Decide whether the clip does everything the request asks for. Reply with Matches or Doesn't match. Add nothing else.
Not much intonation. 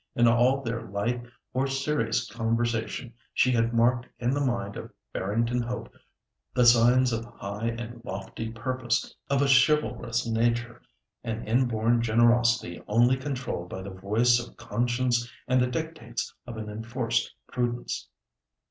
Matches